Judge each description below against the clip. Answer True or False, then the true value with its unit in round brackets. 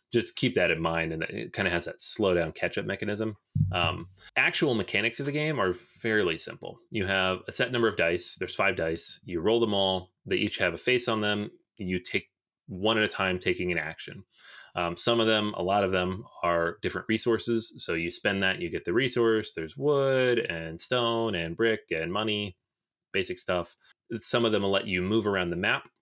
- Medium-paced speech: False (215 wpm)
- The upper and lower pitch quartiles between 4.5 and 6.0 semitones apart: False (3.8 semitones)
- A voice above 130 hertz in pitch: False (105 Hz)